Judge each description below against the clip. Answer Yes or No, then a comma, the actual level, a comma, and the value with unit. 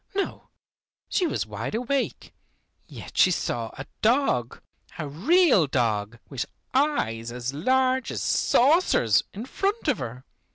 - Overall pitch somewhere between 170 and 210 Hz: No, medium, 160 Hz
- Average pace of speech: No, slow, 130 wpm